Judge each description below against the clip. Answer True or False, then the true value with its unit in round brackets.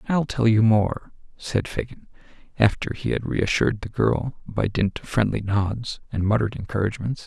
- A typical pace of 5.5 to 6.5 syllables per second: False (5.0 syllables/s)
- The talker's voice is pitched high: False (110 Hz)